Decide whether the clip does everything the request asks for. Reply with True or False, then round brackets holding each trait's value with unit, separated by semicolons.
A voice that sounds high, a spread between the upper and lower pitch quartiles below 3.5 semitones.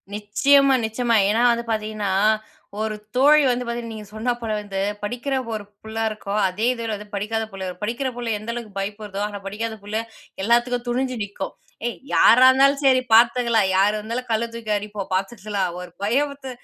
True (225 Hz; 2.8 semitones)